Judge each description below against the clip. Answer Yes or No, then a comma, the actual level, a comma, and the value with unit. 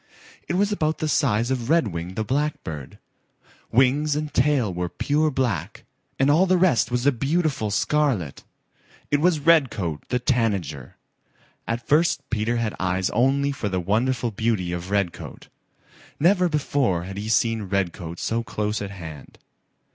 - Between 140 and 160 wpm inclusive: Yes, average, 150 wpm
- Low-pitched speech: Yes, low, 115 Hz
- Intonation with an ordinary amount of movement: No, wide, 6.9 semitones